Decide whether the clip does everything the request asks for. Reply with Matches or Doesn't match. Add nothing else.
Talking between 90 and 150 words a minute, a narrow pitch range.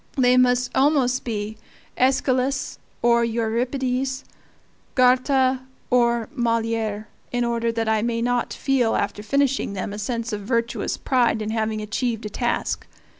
Matches